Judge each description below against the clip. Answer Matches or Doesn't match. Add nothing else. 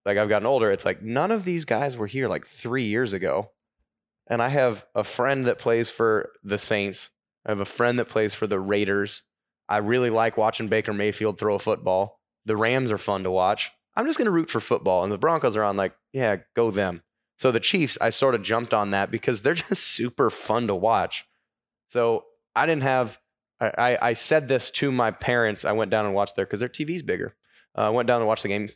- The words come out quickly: Matches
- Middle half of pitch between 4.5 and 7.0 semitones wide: Doesn't match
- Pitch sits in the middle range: Doesn't match